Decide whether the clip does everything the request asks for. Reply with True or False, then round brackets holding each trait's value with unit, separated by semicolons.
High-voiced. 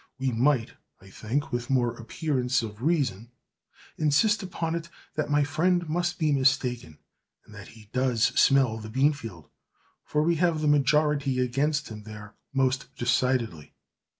False (135 Hz)